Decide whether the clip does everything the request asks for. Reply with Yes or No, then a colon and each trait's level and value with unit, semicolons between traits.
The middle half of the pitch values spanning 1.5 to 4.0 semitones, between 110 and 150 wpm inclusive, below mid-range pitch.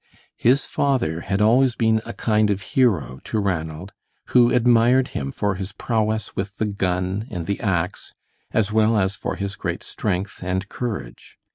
No: average, 3.5 semitones; average, 165 wpm; low, 105 Hz